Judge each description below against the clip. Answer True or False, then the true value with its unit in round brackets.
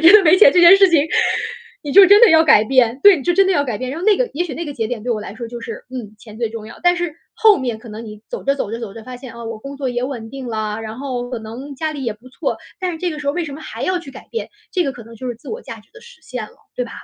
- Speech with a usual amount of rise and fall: False (6.7 semitones)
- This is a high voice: True (260 Hz)